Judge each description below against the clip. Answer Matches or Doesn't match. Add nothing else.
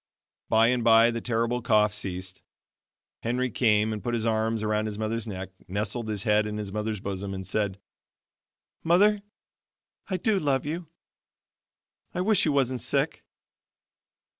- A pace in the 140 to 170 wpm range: Matches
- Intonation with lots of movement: Doesn't match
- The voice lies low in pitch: Matches